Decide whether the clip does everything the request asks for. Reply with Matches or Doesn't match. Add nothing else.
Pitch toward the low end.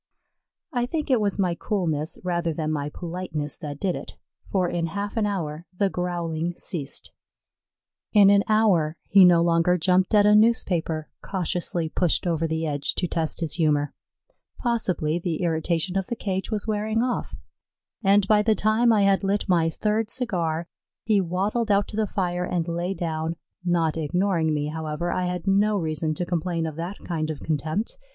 Doesn't match